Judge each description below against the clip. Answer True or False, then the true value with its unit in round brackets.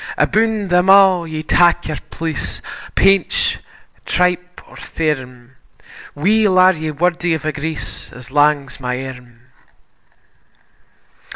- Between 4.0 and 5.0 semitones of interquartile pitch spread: True (4.3 semitones)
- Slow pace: True (115 wpm)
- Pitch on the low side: False (160 Hz)